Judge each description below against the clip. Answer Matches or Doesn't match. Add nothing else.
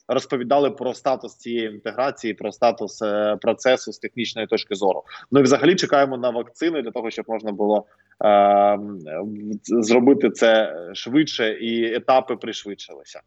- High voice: Doesn't match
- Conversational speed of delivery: Matches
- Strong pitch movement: Doesn't match